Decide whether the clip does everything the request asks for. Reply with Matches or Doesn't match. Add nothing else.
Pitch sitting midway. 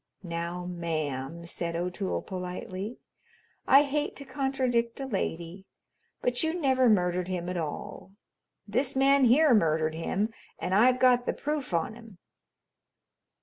Doesn't match